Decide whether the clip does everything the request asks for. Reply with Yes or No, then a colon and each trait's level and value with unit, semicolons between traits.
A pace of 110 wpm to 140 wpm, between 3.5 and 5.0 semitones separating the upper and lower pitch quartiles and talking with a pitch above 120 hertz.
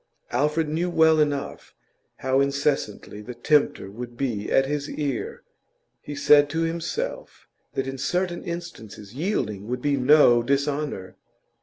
Yes: slow, 135 wpm; average, 3.8 semitones; medium, 140 Hz